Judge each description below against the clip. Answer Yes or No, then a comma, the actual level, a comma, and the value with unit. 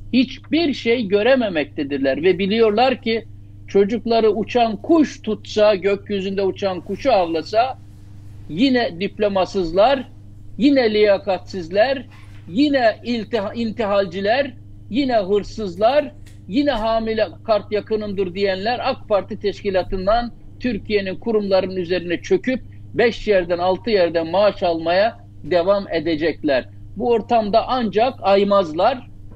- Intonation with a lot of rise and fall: No, average, 4.6 semitones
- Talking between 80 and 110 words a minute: Yes, slow, 95 wpm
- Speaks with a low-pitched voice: No, high, 200 Hz